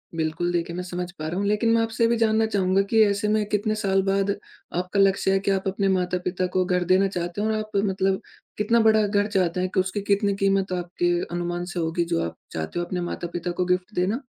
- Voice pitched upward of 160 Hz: Yes, high, 190 Hz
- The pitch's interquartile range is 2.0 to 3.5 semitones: Yes, narrow, 2.4 semitones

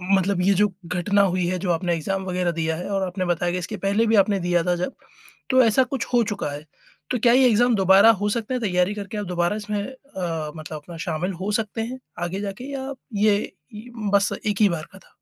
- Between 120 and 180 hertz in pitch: No, high, 195 Hz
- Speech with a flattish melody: No, average, 3.3 semitones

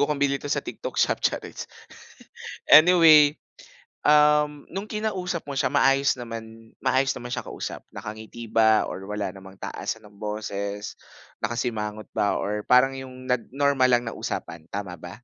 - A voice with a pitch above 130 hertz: No, low, 125 Hz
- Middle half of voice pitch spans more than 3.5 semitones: Yes, average, 5.2 semitones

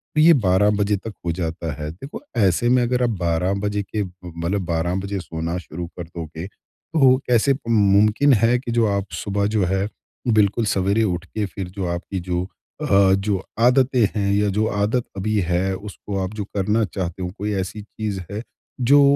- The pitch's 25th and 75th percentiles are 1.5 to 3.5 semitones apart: Yes, average, 3.1 semitones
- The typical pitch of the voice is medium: No, low, 100 Hz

